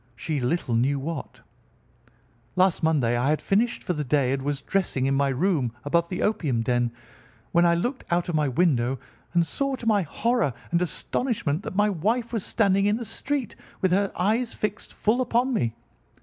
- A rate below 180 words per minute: No, average, 190 wpm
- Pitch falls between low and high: Yes, medium, 175 Hz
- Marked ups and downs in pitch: Yes, wide, 7.2 semitones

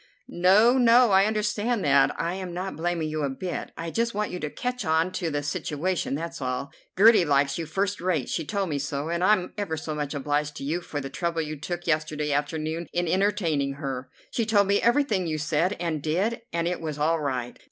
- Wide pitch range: No, average, 4.5 semitones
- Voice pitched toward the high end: No, medium, 165 Hz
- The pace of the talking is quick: Yes, fast, 215 wpm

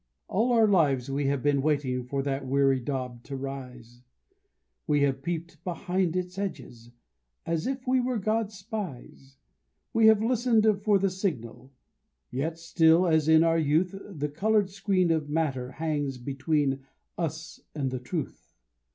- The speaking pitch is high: No, medium, 155 Hz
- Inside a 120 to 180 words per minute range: Yes, average, 150 wpm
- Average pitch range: No, wide, 5.8 semitones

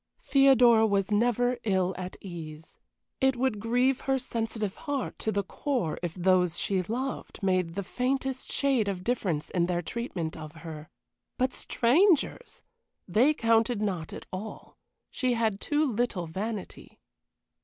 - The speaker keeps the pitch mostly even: No, wide, 5.5 semitones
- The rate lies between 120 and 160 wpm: Yes, average, 145 wpm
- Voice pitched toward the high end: Yes, high, 220 Hz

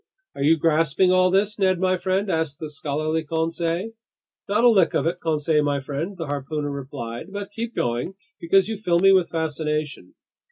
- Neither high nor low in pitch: Yes, medium, 165 Hz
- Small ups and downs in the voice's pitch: No, average, 4.0 semitones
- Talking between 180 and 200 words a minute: Yes, average, 185 wpm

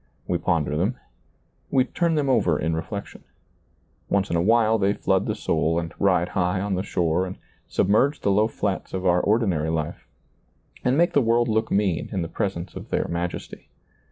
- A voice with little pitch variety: No, average, 4.3 semitones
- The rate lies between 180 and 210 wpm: Yes, average, 185 wpm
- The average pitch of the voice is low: Yes, very low, 95 Hz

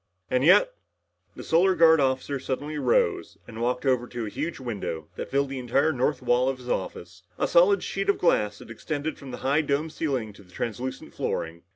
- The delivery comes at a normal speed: No, fast, 210 wpm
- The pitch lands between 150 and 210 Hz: No, low, 135 Hz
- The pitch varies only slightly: No, average, 4.8 semitones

